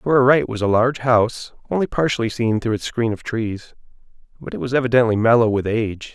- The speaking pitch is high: No, low, 115 Hz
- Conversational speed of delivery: No, fast, 215 wpm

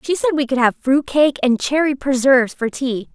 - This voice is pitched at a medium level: No, very high, 270 Hz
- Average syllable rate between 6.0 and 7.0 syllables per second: No, 5.1 syllables/s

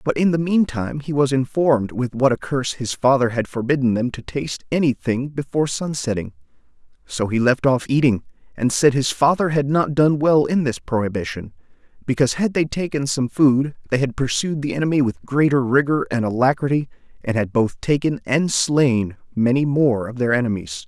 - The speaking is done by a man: Yes, male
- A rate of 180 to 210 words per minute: Yes, average, 195 wpm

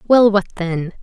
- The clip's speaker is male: No, female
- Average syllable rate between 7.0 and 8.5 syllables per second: No, 4.4 syllables/s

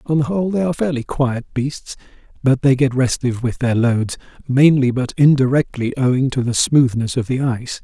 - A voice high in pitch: No, low, 130 Hz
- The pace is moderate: Yes, average, 190 wpm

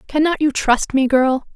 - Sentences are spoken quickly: No, average, 195 wpm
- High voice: Yes, very high, 275 Hz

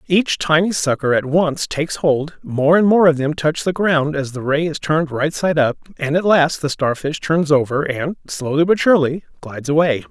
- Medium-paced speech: No, fast, 215 wpm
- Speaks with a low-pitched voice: No, medium, 155 Hz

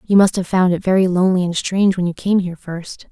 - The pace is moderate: No, fast, 270 wpm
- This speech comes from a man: No, female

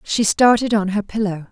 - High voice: Yes, high, 205 Hz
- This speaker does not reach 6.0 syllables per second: Yes, 5.0 syllables/s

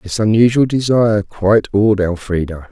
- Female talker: No, male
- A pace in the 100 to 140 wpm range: Yes, slow, 135 wpm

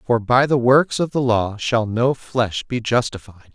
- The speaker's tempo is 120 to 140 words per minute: No, fast, 205 wpm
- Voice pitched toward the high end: No, low, 120 Hz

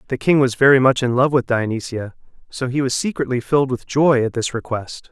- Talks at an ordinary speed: No, fast, 225 wpm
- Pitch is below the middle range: Yes, low, 130 Hz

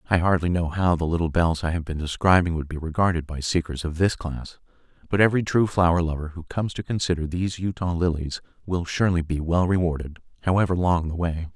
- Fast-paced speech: Yes, fast, 210 wpm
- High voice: No, very low, 85 Hz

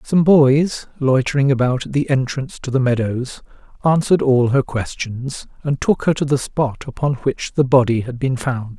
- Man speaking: Yes, male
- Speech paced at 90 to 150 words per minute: No, average, 185 wpm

